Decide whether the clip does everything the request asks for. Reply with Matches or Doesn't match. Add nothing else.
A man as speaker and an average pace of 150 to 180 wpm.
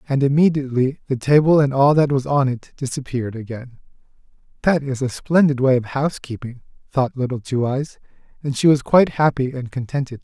Matches